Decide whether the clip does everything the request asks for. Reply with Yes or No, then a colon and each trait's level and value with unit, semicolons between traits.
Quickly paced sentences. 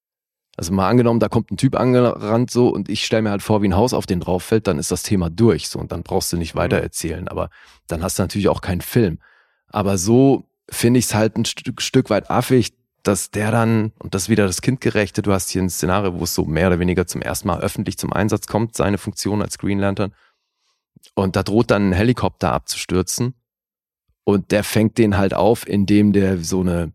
Yes: fast, 230 wpm